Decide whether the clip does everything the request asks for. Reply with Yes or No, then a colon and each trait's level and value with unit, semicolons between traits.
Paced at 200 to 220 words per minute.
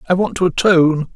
Yes: fast, 205 wpm